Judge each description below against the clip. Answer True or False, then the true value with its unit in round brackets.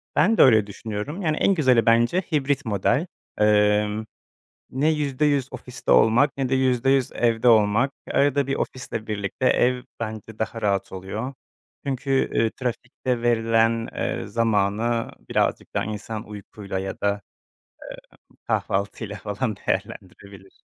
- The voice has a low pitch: True (115 Hz)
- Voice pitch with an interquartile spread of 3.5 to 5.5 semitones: True (4.0 semitones)